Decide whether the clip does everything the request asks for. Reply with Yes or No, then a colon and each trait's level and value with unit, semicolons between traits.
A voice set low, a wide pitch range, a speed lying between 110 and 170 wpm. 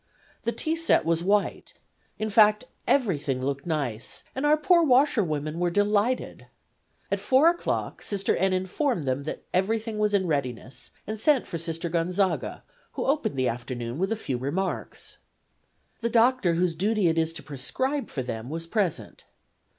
No: medium, 185 Hz; wide, 6.7 semitones; average, 160 wpm